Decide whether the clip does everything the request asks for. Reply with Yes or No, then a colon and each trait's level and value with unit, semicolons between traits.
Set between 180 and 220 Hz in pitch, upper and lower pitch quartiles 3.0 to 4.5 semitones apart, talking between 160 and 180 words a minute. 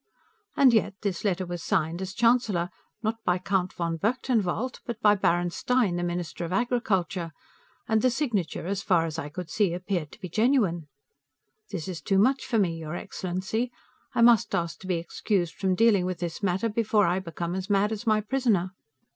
No: high, 190 Hz; average, 4.2 semitones; average, 190 wpm